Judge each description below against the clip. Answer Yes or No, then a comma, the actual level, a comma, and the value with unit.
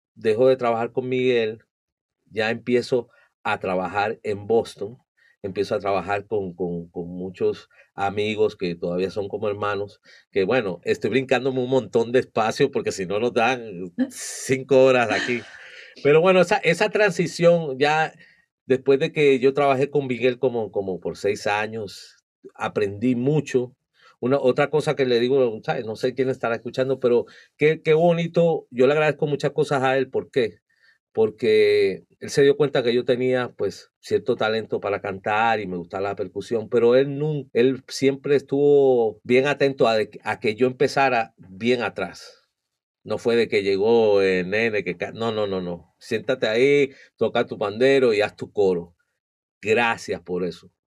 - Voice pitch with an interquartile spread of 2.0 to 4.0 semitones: No, average, 4.8 semitones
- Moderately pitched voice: No, low, 130 Hz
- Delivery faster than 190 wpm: No, average, 165 wpm